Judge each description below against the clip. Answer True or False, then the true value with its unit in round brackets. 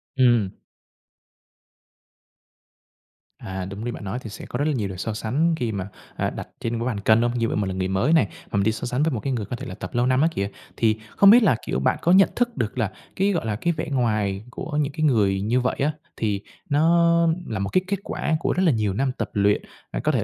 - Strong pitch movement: True (6.6 semitones)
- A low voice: True (120 Hz)